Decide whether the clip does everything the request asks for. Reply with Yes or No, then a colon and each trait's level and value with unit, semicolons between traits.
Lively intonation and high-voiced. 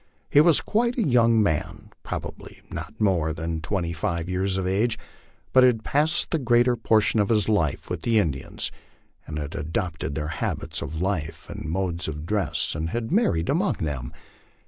No: wide, 6.3 semitones; very low, 95 Hz